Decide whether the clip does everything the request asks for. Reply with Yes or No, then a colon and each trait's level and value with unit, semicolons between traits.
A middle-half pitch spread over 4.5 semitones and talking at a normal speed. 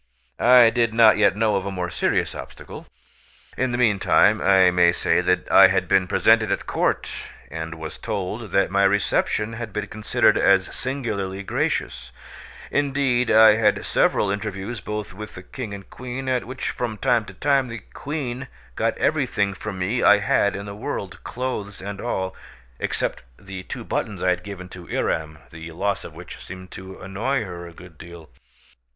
No: average, 3.7 semitones; average, 180 wpm